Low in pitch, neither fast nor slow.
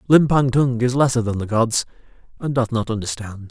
Yes: low, 120 Hz; average, 190 wpm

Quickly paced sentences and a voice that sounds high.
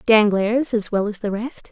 Yes: fast, 210 wpm; high, 215 Hz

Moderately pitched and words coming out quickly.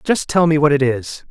Yes: medium, 150 Hz; fast, 275 wpm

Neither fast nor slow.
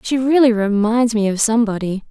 Yes: average, 170 wpm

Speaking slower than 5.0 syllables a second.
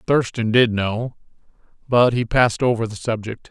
Yes: 4.8 syllables/s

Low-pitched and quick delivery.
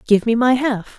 No: high, 235 Hz; fast, 245 wpm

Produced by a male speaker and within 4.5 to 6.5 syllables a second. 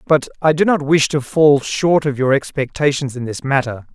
Yes: male; 5.0 syllables/s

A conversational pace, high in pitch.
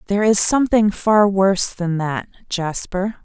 Yes: average, 150 wpm; high, 200 Hz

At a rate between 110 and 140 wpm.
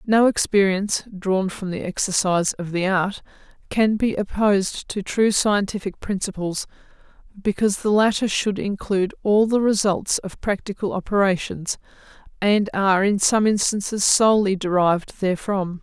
Yes: slow, 135 wpm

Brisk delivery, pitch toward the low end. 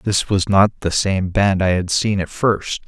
Yes: fast, 230 wpm; very low, 95 Hz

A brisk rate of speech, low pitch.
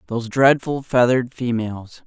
No: slow, 115 wpm; low, 125 Hz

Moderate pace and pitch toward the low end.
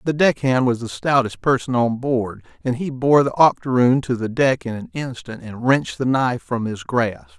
No: fast, 210 wpm; low, 125 Hz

